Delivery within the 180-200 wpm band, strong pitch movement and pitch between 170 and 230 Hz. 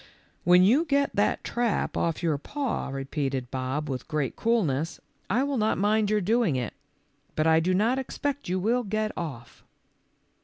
Yes: average, 185 wpm; wide, 7.7 semitones; medium, 185 Hz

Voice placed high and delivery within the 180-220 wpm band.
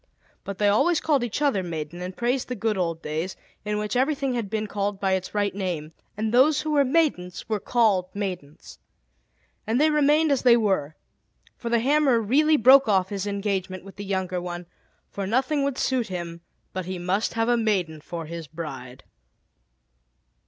Yes: high, 205 Hz; average, 185 wpm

